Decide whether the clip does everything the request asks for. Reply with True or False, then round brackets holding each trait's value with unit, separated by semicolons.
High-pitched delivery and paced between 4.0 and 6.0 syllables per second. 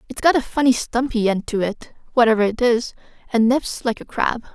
True (235 Hz; 5.4 syllables/s)